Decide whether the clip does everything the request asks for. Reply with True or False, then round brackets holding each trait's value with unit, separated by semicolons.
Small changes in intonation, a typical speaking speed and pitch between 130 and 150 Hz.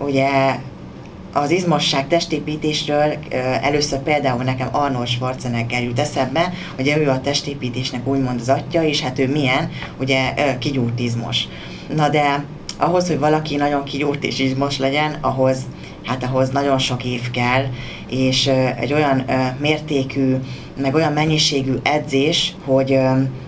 True (2.2 semitones; 130 wpm; 135 Hz)